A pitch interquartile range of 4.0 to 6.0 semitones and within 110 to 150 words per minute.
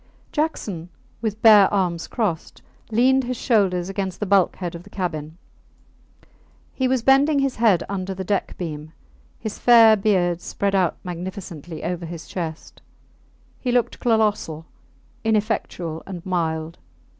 Yes: average, 4.4 semitones; slow, 135 wpm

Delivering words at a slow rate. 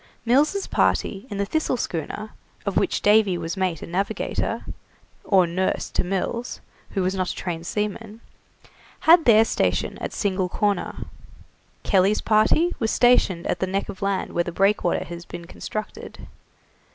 No: average, 155 wpm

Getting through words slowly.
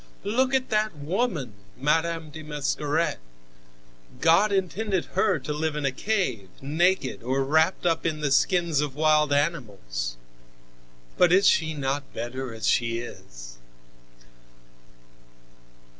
Yes: slow, 125 wpm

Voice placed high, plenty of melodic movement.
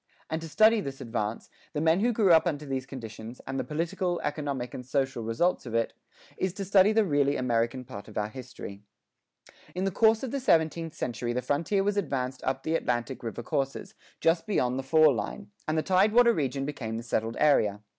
No: medium, 145 Hz; wide, 6.4 semitones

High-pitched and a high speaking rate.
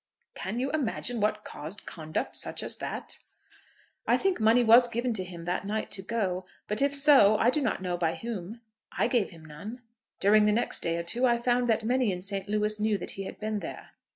Yes: high, 215 Hz; fast, 220 wpm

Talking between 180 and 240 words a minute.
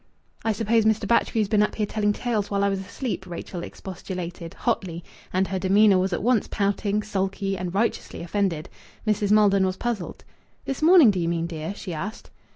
Yes: average, 185 wpm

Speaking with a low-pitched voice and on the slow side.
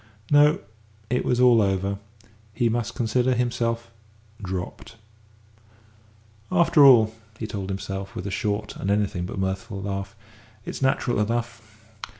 Yes: low, 110 Hz; slow, 130 wpm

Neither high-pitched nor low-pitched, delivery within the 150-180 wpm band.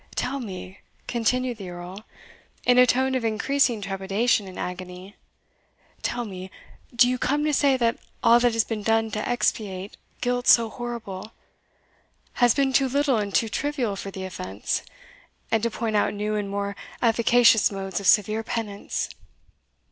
No: high, 225 Hz; average, 160 wpm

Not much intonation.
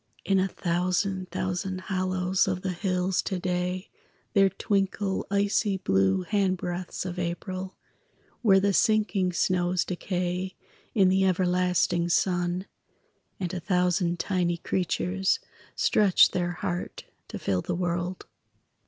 Yes: narrow, 1.4 semitones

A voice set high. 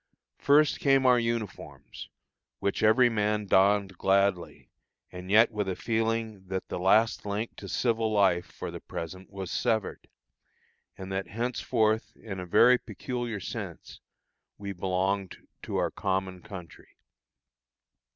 No: low, 105 Hz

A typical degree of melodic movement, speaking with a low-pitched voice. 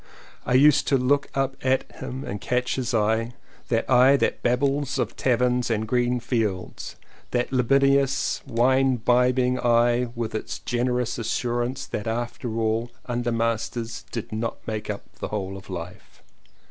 No: narrow, 2.0 semitones; low, 120 Hz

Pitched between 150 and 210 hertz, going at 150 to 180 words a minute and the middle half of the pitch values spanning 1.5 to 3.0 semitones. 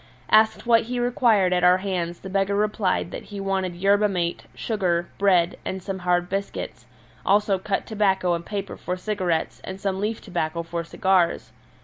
Yes: high, 190 Hz; average, 170 wpm; narrow, 2.5 semitones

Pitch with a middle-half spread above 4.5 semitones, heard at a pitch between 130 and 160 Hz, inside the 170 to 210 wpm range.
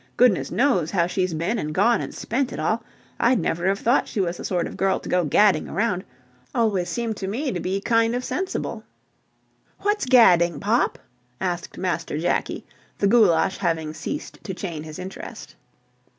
No: average, 5.1 semitones; high, 190 Hz; average, 180 wpm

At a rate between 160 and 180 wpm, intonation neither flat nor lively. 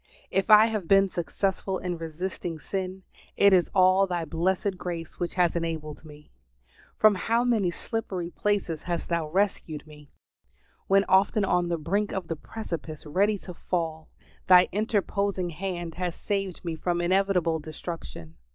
No: average, 150 wpm; average, 3.0 semitones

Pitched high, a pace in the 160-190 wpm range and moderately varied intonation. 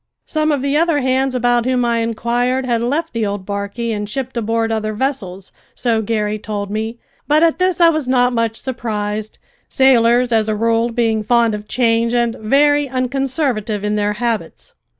Yes: high, 235 Hz; average, 180 wpm; average, 3.2 semitones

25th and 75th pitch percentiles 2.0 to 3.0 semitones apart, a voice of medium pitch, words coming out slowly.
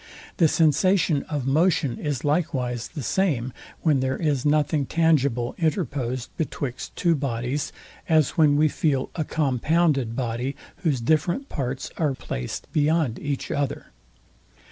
No: average, 3.6 semitones; medium, 145 Hz; slow, 130 wpm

